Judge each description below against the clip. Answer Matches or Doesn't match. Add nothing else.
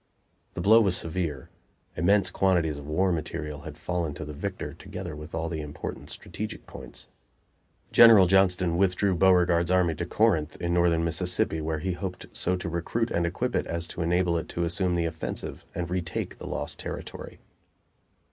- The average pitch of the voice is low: Matches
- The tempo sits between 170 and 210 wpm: Matches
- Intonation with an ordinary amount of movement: Doesn't match